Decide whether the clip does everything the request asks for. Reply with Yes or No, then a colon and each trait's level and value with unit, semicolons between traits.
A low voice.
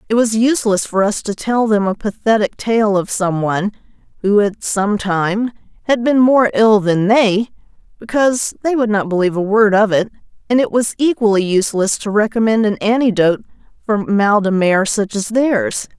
No: high, 210 Hz